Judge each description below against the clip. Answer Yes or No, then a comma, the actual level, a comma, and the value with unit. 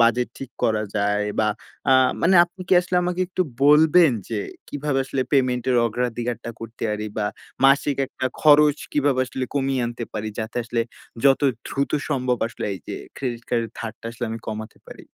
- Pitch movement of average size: Yes, average, 3.9 semitones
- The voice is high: No, low, 125 Hz